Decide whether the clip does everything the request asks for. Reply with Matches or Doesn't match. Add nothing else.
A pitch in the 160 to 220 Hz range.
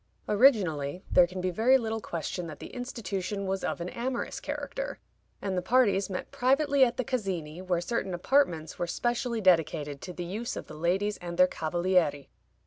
Matches